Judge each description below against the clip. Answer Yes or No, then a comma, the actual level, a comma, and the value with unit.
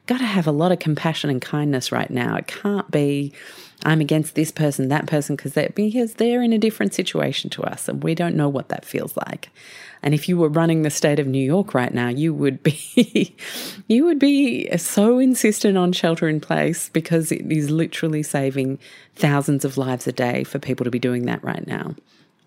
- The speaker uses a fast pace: Yes, fast, 215 wpm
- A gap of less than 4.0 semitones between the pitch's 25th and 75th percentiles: No, average, 4.5 semitones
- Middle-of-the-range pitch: Yes, medium, 155 Hz